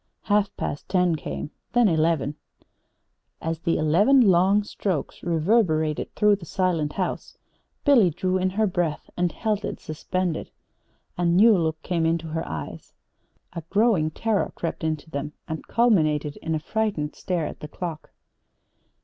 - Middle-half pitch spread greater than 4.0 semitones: Yes, average, 4.4 semitones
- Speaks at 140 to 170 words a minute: Yes, average, 150 wpm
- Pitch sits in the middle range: Yes, medium, 170 Hz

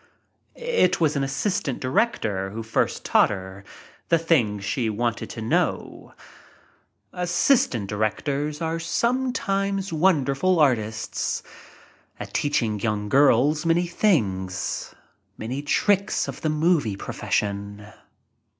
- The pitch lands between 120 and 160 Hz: Yes, medium, 140 Hz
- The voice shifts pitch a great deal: Yes, wide, 8.2 semitones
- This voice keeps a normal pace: No, slow, 115 wpm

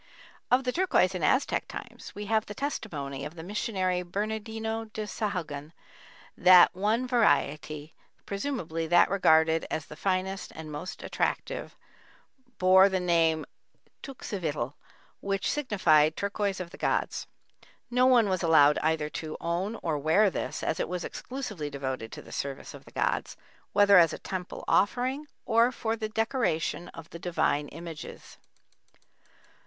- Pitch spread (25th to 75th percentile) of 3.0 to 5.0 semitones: No, wide, 5.4 semitones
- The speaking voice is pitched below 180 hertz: No, medium, 185 Hz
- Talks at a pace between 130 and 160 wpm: Yes, average, 145 wpm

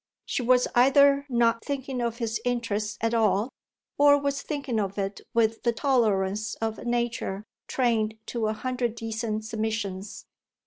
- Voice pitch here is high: Yes, high, 230 Hz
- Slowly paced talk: No, average, 150 wpm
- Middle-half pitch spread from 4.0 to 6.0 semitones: No, narrow, 2.6 semitones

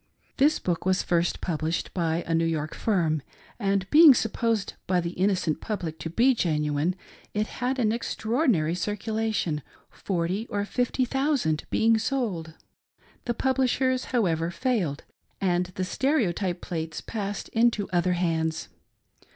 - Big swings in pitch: Yes, wide, 5.7 semitones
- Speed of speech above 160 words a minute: No, average, 140 wpm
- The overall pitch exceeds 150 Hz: Yes, high, 190 Hz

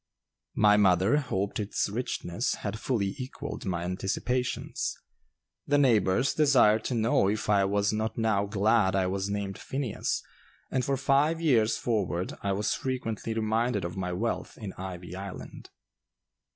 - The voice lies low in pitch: Yes, low, 105 Hz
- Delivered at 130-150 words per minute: Yes, average, 145 wpm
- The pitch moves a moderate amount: Yes, average, 4.1 semitones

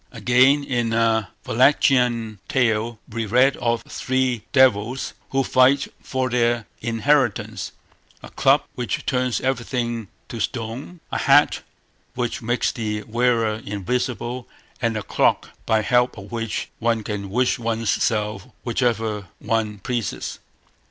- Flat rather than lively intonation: Yes, narrow, 2.3 semitones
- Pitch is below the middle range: Yes, low, 115 Hz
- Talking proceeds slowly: Yes, slow, 125 wpm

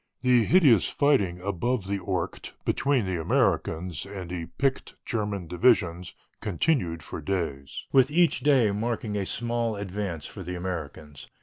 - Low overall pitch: Yes, low, 100 Hz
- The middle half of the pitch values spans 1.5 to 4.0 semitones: No, average, 5.3 semitones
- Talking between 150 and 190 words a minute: No, average, 140 wpm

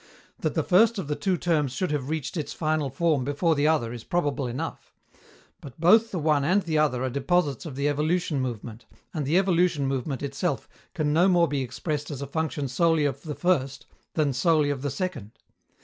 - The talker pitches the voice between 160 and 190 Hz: No, medium, 150 Hz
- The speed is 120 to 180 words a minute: No, fast, 205 wpm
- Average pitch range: Yes, average, 3.7 semitones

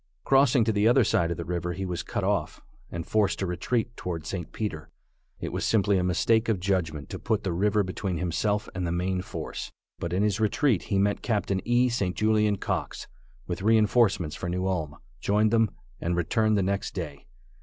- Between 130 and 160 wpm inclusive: No, average, 200 wpm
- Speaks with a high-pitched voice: No, low, 100 Hz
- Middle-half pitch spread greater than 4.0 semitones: No, average, 3.6 semitones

